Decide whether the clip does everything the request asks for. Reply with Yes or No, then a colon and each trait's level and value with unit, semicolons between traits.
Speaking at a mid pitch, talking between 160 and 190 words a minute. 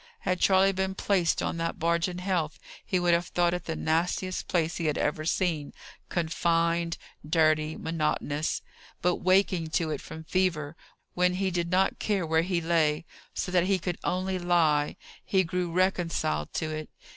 Yes: medium, 170 Hz; average, 170 wpm